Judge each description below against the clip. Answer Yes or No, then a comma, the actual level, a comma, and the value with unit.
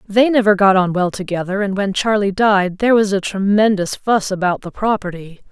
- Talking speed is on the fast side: No, average, 195 wpm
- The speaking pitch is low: No, high, 200 Hz